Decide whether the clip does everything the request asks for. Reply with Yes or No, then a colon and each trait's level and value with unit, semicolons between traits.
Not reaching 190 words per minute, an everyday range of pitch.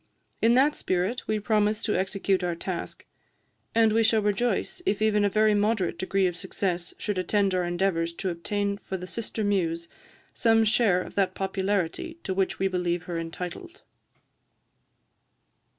Yes: average, 160 wpm; average, 3.1 semitones